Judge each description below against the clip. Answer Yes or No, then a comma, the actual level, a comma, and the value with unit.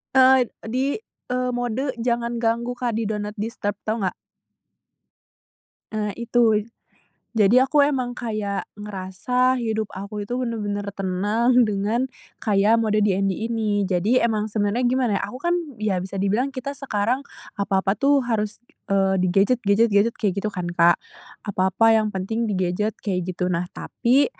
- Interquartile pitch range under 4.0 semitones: Yes, average, 3.3 semitones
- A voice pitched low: No, high, 215 Hz